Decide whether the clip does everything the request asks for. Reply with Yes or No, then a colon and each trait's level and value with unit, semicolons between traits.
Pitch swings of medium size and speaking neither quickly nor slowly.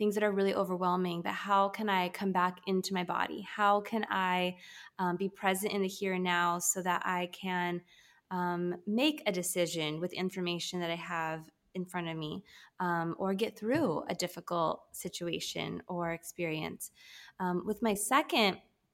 No: narrow, 2.1 semitones; average, 175 wpm